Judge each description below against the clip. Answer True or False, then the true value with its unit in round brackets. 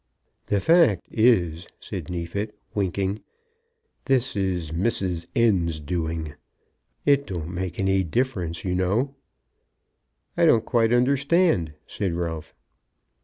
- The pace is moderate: False (110 wpm)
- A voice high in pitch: False (95 Hz)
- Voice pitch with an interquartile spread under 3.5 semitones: False (5.6 semitones)